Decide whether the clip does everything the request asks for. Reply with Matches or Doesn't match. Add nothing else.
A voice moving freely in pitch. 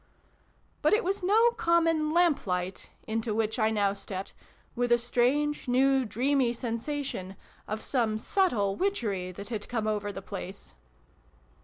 Matches